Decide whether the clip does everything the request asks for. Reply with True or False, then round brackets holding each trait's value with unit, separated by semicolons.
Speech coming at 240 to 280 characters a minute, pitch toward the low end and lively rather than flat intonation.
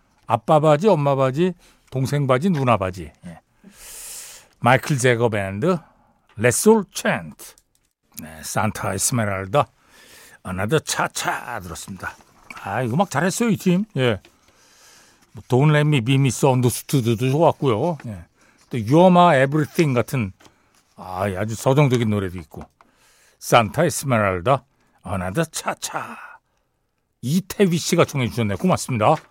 True (260 characters per minute; 130 Hz; 6.4 semitones)